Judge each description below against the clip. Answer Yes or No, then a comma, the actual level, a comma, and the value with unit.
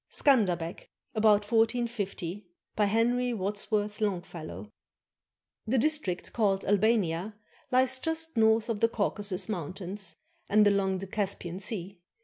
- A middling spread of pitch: Yes, average, 3.3 semitones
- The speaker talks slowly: Yes, slow, 115 wpm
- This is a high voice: Yes, high, 205 Hz